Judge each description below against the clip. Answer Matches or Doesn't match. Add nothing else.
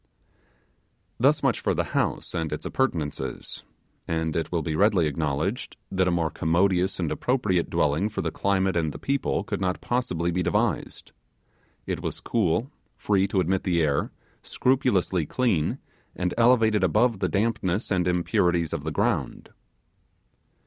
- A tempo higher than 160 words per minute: Doesn't match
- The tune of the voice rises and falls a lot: Doesn't match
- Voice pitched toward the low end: Matches